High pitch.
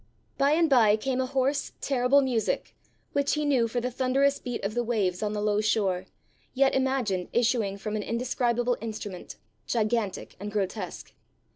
Yes: high, 235 Hz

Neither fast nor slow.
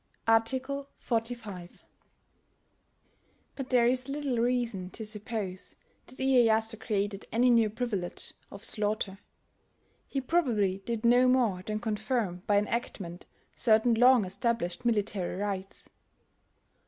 No: slow, 110 wpm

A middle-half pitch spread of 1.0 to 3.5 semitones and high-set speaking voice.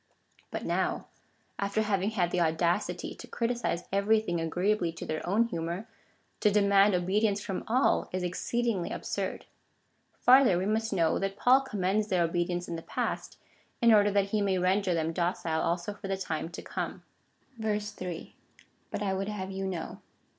Yes: average, 3.2 semitones; high, 195 Hz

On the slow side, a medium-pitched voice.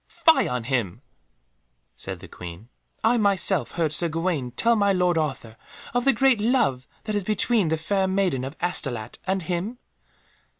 No: average, 165 wpm; medium, 180 Hz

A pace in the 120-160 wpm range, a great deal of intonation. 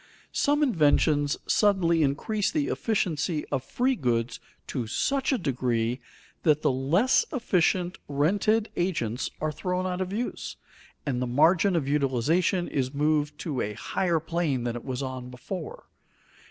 Yes: average, 145 wpm; wide, 6.1 semitones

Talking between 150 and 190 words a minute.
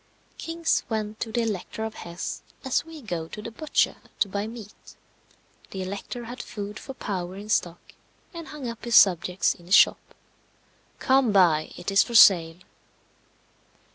Yes: average, 165 wpm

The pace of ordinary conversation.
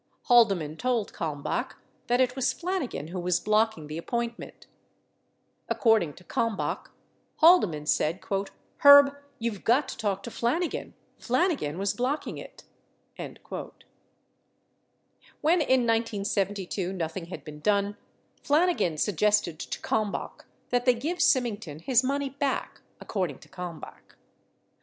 No: slow, 125 wpm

